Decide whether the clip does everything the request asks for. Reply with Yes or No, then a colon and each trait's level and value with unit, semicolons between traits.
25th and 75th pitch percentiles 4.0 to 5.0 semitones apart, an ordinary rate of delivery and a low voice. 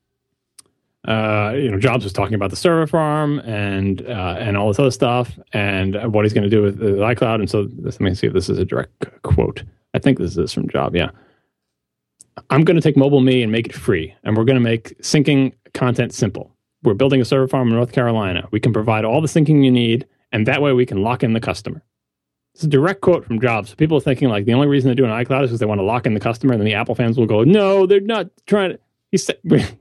No: average, 4.3 semitones; fast, 255 wpm; low, 125 Hz